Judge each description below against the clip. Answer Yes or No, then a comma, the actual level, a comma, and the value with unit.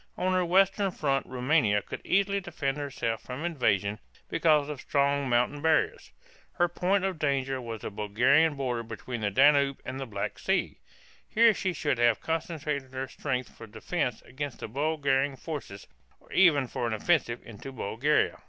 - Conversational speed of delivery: Yes, average, 165 wpm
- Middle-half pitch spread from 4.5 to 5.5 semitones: Yes, average, 4.8 semitones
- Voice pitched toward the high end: No, medium, 140 Hz